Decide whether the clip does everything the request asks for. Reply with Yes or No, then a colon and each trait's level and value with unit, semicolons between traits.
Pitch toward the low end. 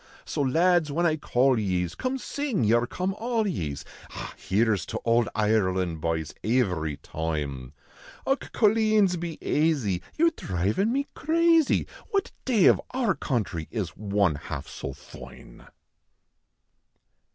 Yes: low, 120 Hz